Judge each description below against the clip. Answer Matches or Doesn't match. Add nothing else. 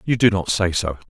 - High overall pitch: Doesn't match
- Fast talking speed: Matches